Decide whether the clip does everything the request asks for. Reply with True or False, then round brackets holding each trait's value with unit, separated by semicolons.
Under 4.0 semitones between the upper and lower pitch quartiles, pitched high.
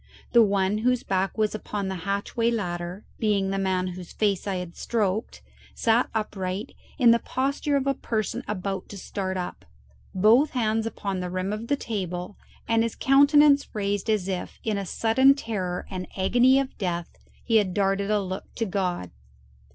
True (3.5 semitones; 205 Hz)